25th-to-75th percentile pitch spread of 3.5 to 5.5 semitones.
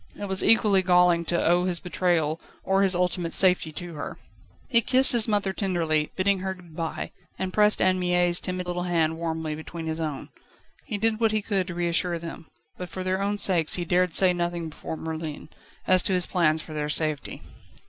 No: narrow, 2.5 semitones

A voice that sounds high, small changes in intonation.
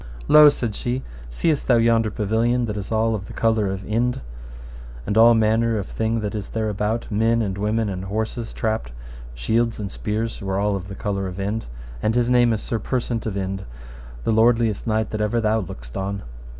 No: low, 110 Hz; narrow, 2.3 semitones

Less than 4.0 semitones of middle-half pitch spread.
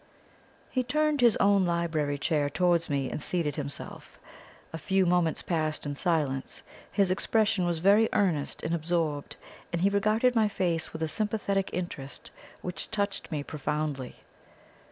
No: average, 4.7 semitones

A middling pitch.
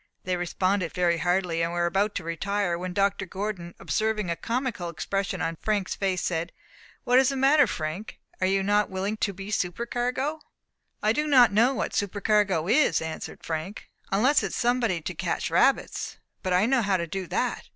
No: high, 195 Hz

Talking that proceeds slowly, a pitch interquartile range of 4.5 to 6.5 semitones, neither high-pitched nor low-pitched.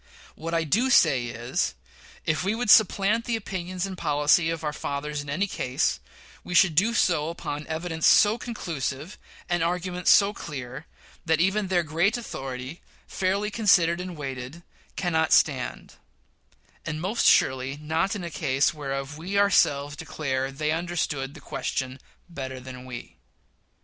No: average, 155 wpm; average, 4.8 semitones; medium, 160 Hz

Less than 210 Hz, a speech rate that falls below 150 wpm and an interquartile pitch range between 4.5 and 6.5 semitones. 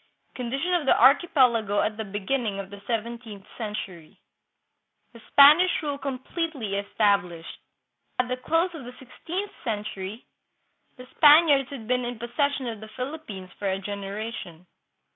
No: high, 235 Hz; average, 140 wpm; average, 5.3 semitones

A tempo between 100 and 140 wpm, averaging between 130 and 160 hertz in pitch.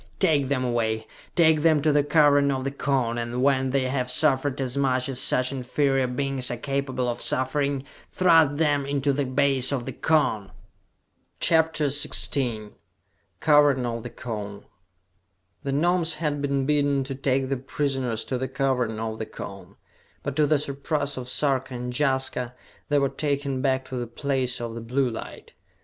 No: average, 170 wpm; low, 135 Hz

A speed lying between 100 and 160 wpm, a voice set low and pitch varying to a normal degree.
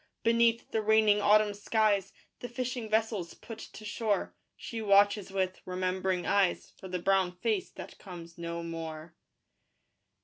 No: average, 140 wpm; high, 200 Hz; average, 3.2 semitones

